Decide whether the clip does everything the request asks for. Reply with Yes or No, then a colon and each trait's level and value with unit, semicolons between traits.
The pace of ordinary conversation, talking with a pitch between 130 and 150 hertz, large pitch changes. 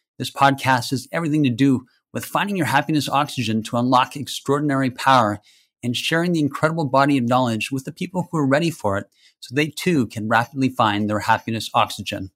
No: average, 190 wpm; low, 135 Hz; average, 4.2 semitones